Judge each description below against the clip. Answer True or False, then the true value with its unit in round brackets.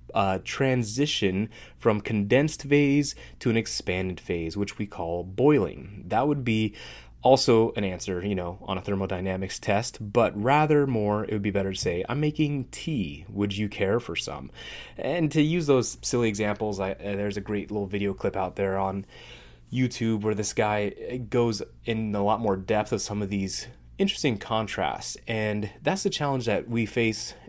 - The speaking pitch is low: True (105 Hz)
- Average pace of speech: True (180 wpm)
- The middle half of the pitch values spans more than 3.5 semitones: True (3.9 semitones)